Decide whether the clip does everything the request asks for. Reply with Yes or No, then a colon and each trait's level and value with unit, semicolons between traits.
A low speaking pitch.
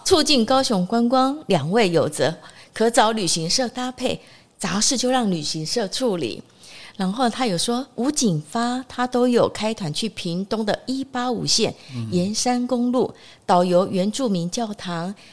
No: high, 225 Hz